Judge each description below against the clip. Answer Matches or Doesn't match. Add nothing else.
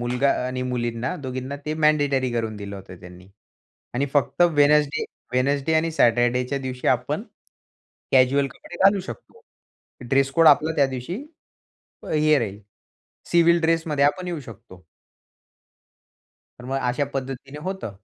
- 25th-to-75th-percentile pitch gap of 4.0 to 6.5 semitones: Doesn't match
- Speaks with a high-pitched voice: Doesn't match